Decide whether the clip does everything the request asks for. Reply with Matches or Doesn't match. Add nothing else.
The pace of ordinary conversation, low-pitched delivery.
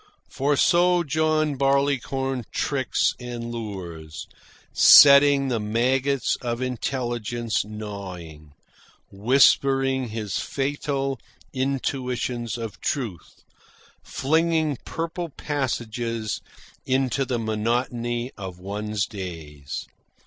Doesn't match